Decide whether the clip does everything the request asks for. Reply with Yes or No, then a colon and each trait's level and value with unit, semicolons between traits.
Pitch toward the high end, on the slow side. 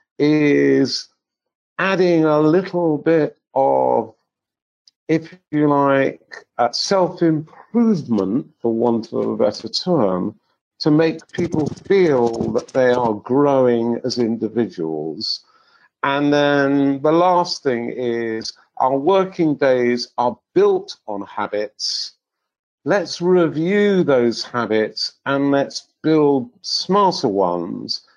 No: medium, 140 Hz; slow, 105 wpm